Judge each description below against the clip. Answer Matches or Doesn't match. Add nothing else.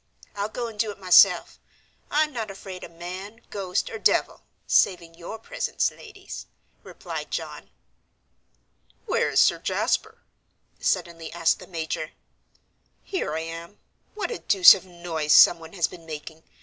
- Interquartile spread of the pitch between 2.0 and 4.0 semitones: Doesn't match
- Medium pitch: Matches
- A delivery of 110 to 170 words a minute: Matches